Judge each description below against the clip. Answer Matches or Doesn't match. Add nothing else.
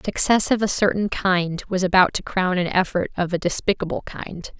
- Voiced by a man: Doesn't match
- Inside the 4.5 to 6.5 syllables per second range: Matches